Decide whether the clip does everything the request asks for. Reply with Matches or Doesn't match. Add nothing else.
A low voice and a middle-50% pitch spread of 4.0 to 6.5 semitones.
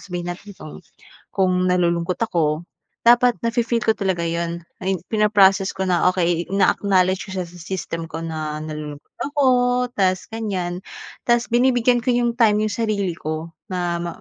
Doesn't match